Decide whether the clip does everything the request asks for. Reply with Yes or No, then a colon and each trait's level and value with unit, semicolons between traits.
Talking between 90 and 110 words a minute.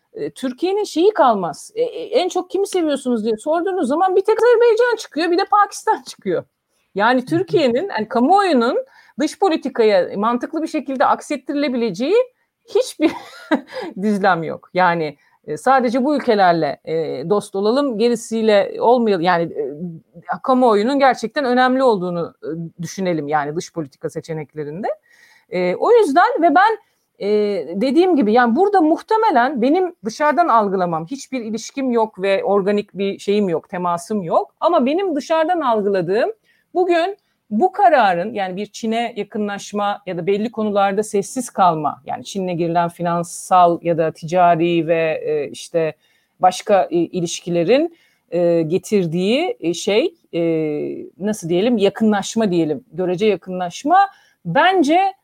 No: average, 120 wpm